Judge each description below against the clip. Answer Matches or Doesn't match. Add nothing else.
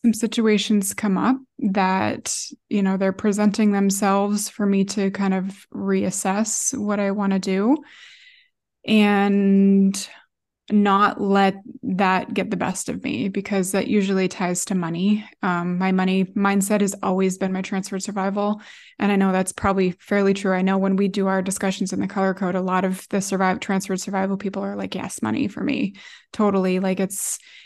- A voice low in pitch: Doesn't match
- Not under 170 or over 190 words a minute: Matches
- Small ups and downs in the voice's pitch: Matches